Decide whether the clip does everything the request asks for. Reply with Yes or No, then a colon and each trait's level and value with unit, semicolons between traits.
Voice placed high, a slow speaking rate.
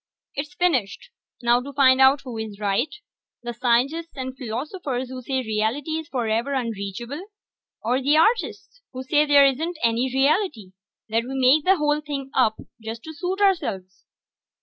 No: very high, 260 Hz; average, 155 wpm